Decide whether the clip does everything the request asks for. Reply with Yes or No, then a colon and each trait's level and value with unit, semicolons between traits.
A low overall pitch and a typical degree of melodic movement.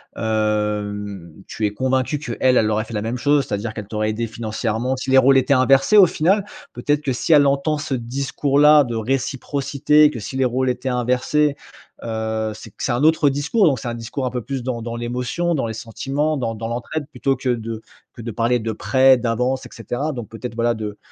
Yes: low, 125 Hz; average, 3.6 semitones